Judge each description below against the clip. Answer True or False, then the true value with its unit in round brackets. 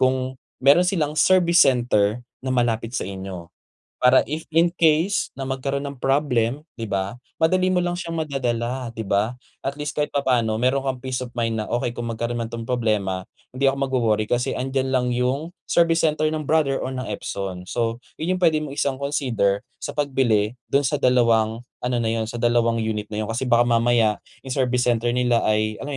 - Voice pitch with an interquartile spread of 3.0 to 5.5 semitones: True (3.5 semitones)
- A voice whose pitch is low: True (125 Hz)